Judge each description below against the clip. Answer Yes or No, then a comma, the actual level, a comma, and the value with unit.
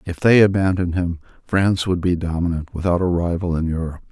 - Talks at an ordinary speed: Yes, average, 190 wpm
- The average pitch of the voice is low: Yes, very low, 90 Hz